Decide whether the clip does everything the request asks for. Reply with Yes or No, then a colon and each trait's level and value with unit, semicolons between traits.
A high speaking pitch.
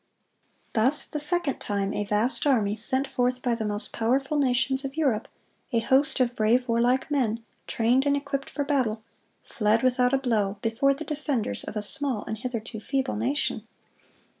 Yes: very high, 250 Hz